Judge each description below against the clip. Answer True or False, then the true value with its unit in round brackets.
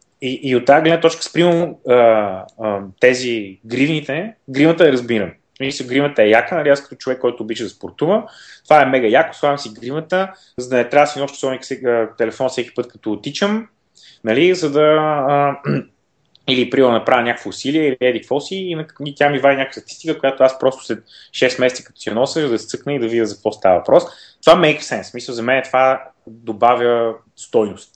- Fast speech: True (205 wpm)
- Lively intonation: False (3.4 semitones)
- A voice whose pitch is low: True (130 Hz)